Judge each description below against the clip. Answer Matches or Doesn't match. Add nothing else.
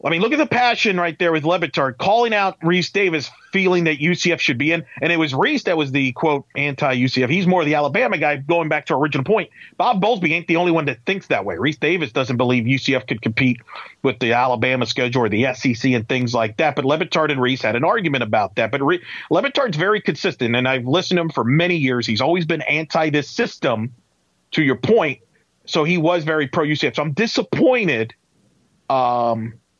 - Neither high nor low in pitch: Matches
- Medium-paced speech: Doesn't match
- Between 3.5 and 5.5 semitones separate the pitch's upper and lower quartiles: Matches